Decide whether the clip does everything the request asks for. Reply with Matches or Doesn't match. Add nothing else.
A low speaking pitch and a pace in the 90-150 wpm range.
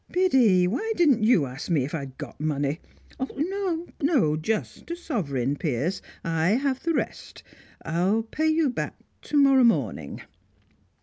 Doesn't match